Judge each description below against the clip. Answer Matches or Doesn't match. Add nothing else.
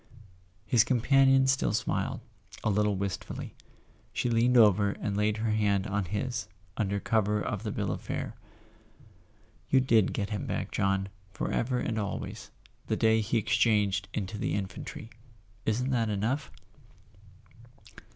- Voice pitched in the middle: Doesn't match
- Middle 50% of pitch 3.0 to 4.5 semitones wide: Doesn't match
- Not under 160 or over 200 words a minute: Doesn't match